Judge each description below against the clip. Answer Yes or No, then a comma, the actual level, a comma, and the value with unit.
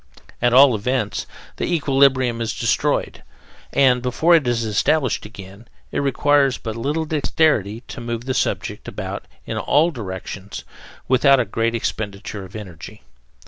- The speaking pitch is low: Yes, low, 120 Hz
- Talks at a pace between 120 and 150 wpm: Yes, average, 140 wpm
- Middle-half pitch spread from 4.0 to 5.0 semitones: Yes, average, 4.3 semitones